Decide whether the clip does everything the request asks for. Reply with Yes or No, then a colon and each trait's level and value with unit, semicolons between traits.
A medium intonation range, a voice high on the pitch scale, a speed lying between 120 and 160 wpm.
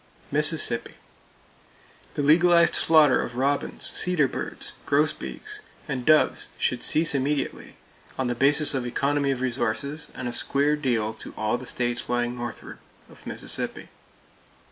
No: average, 3.5 semitones; medium, 140 Hz; slow, 135 wpm